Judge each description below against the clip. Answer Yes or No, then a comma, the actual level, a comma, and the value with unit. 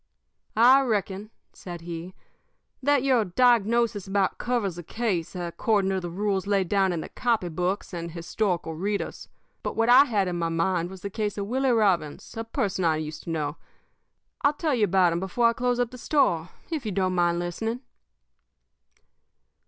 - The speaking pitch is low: No, high, 195 Hz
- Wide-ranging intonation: No, average, 4.9 semitones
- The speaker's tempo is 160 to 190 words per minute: Yes, average, 180 wpm